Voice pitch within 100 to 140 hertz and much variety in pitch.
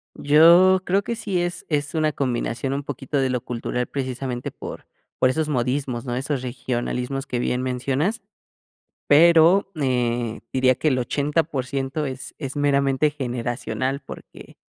No: low, 135 Hz; average, 3.2 semitones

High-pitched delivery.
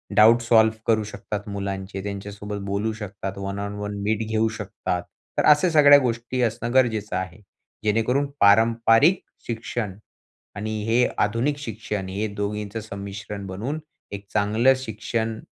No: low, 110 Hz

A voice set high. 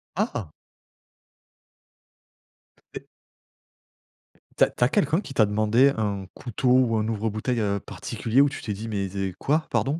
No: low, 115 Hz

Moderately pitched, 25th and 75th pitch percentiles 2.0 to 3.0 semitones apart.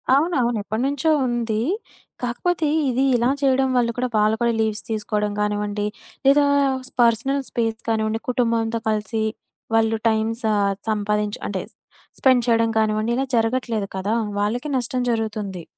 No: high, 225 Hz; narrow, 2.5 semitones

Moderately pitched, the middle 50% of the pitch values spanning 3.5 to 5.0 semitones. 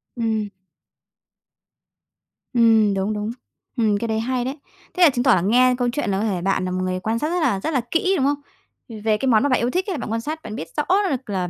No: high, 230 Hz; average, 4.3 semitones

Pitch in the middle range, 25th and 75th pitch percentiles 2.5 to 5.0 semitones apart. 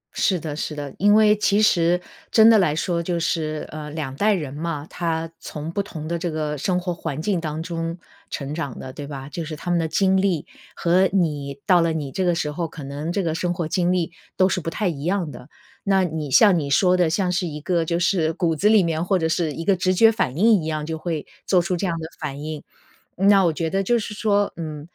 Yes: medium, 170 Hz; average, 3.3 semitones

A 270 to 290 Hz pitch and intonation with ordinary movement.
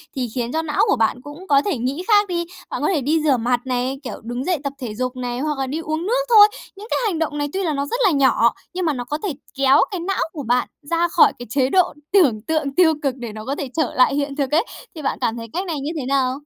Yes: very high, 285 Hz; average, 4.7 semitones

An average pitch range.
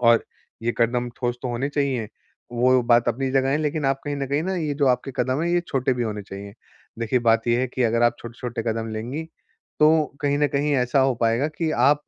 Yes: average, 3.2 semitones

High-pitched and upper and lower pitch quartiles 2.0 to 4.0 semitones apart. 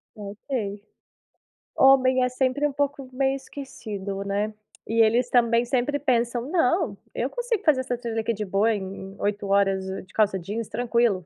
No: high, 235 Hz; average, 4.5 semitones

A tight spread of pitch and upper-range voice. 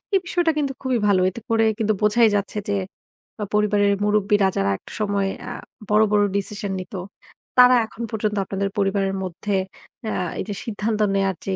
Yes: narrow, 1.8 semitones; high, 210 Hz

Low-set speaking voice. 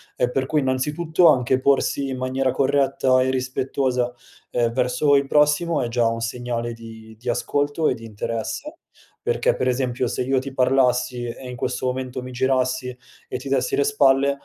Yes: low, 130 Hz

